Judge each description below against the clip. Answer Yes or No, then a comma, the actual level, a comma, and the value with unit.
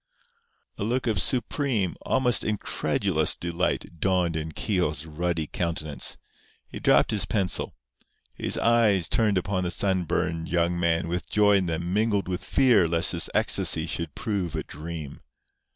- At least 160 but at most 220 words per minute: No, average, 145 wpm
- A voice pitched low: Yes, very low, 90 Hz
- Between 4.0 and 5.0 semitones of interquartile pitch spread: No, average, 3.6 semitones